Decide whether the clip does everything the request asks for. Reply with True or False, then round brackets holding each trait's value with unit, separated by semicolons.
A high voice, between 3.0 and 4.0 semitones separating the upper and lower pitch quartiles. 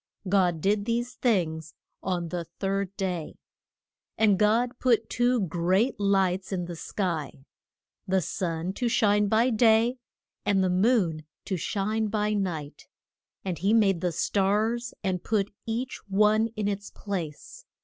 True (200 Hz; 3.4 semitones)